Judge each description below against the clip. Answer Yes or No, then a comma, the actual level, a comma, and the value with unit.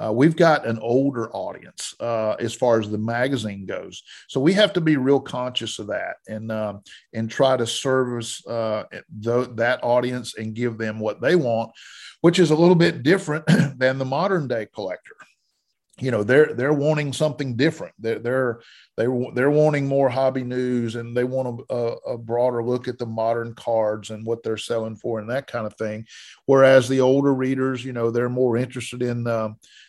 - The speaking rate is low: No, average, 195 wpm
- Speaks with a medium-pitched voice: No, low, 125 Hz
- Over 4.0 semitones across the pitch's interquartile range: No, average, 2.8 semitones